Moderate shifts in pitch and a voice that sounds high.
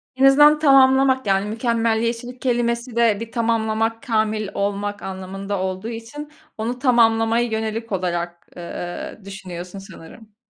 Yes: average, 3.2 semitones; high, 225 Hz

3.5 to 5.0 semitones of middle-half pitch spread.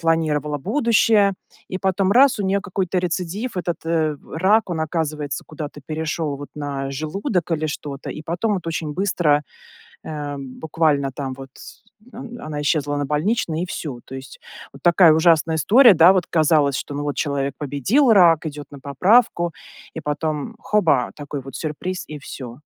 Yes: average, 4.1 semitones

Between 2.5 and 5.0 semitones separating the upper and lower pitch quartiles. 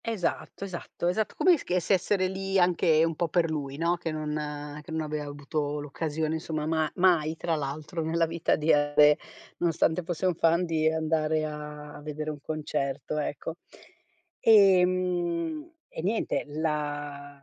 Yes: average, 2.8 semitones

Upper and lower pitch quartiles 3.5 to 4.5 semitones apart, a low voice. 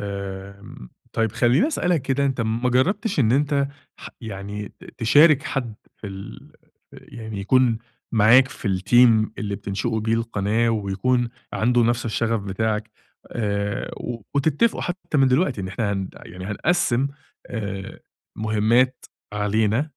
Yes: average, 3.9 semitones; low, 115 Hz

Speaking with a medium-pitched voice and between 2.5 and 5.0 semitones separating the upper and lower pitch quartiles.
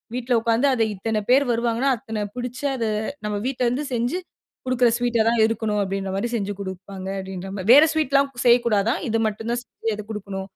No: high, 230 Hz; average, 3.4 semitones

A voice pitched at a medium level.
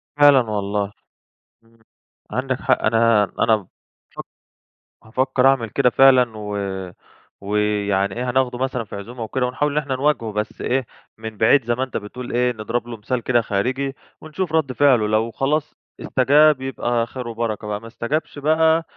No: low, 125 Hz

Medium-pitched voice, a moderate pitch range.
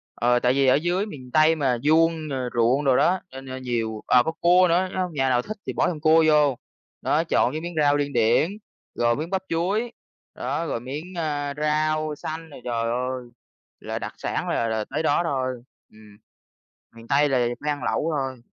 Yes: medium, 145 Hz; average, 4.4 semitones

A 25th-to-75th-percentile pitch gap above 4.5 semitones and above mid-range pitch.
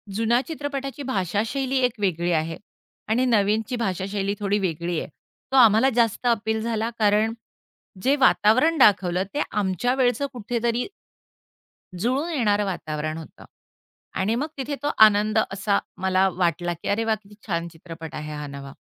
Yes: average, 4.9 semitones; high, 210 Hz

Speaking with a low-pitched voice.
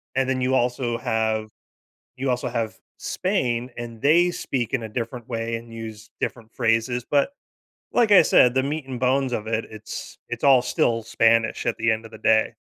Yes: low, 120 Hz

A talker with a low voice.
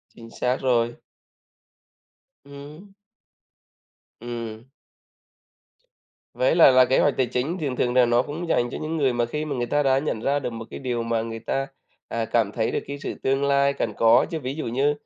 Yes: low, 130 Hz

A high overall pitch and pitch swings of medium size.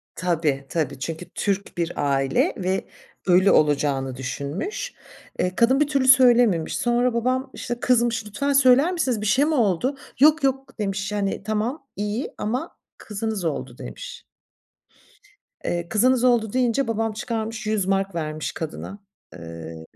No: high, 215 Hz; wide, 6.7 semitones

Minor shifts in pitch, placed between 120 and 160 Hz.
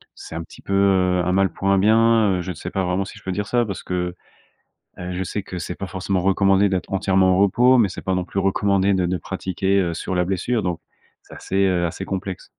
No: narrow, 1.4 semitones; very low, 95 Hz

